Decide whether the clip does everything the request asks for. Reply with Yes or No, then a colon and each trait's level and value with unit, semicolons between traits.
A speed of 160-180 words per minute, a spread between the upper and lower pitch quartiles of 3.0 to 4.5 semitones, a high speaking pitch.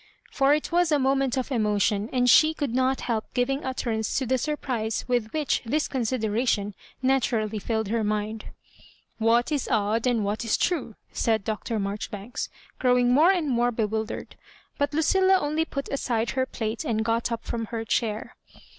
Yes: average, 175 wpm; average, 3.6 semitones; high, 240 Hz